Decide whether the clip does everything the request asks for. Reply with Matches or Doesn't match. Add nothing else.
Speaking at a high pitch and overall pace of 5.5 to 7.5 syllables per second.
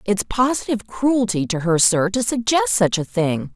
Doesn't match